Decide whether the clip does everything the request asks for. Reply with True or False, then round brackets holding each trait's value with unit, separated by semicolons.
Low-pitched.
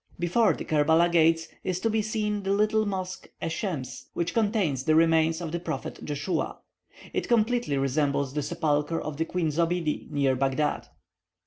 False (165 Hz)